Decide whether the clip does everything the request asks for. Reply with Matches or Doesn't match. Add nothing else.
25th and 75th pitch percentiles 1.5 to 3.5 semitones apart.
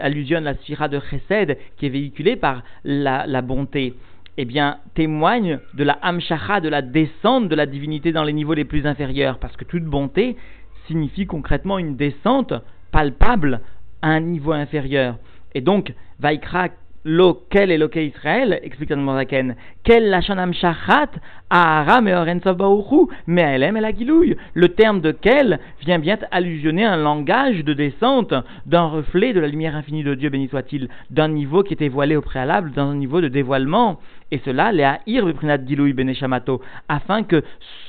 Doesn't match